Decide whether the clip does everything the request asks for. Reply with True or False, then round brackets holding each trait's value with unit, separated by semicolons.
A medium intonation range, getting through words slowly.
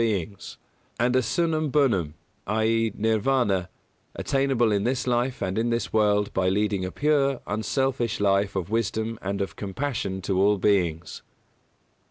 True (4.1 semitones; 120 wpm)